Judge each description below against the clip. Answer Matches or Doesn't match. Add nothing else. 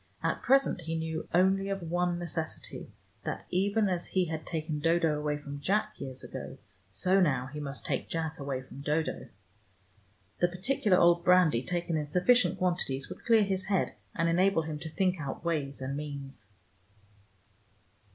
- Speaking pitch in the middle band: Matches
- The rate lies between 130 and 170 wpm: Matches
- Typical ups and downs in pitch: Matches